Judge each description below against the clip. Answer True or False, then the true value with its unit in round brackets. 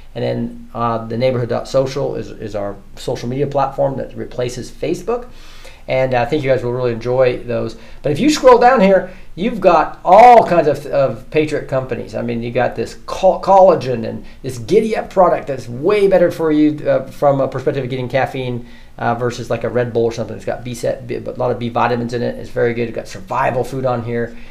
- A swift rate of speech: True (215 wpm)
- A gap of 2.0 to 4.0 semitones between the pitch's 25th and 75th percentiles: False (4.4 semitones)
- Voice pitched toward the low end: True (130 Hz)